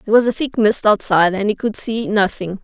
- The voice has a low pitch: No, high, 210 Hz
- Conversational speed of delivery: No, fast, 250 wpm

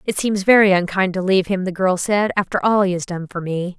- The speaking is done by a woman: Yes, female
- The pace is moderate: No, fast, 270 wpm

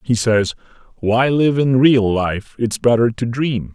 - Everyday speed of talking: Yes, average, 175 wpm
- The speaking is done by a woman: No, male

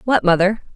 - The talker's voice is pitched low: No, high, 200 Hz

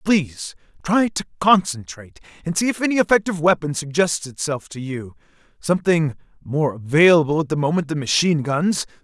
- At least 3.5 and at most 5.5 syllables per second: No, 5.7 syllables/s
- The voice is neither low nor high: Yes, medium, 160 Hz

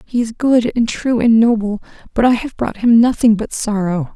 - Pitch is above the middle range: Yes, high, 230 Hz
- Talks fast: Yes, fast, 215 wpm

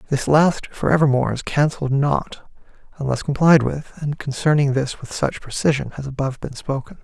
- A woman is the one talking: No, male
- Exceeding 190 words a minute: No, average, 170 wpm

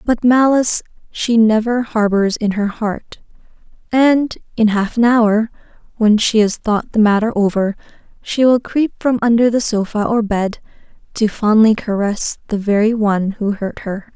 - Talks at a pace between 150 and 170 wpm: Yes, average, 160 wpm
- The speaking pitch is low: No, high, 220 Hz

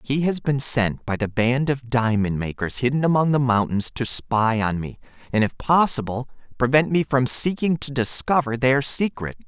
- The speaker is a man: Yes, male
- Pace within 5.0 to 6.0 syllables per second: No, 4.7 syllables/s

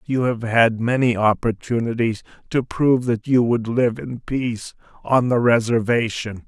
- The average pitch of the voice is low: Yes, low, 120 Hz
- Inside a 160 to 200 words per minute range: No, average, 150 wpm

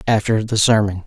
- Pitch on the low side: Yes, low, 105 Hz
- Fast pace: No, average, 170 wpm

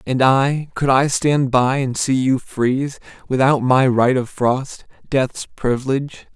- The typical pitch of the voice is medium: No, low, 130 Hz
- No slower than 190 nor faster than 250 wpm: No, average, 160 wpm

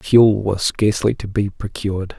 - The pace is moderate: Yes, average, 165 wpm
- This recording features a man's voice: Yes, male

